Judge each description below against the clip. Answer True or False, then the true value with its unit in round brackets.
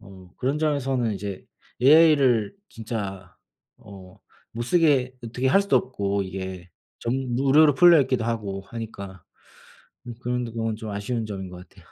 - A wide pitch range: False (5.0 semitones)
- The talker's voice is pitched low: True (115 Hz)